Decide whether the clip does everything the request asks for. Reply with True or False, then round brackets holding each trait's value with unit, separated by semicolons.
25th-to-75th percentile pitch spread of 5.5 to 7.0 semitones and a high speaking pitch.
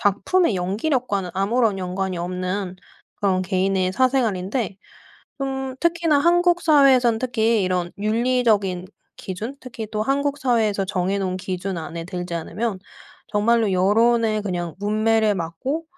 False (5.1 semitones; 210 Hz)